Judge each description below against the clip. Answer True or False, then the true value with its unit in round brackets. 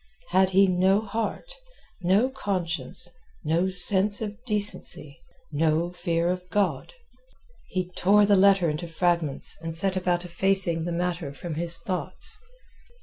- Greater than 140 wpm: False (135 wpm)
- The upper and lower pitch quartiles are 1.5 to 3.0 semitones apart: True (2.6 semitones)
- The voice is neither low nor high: True (180 Hz)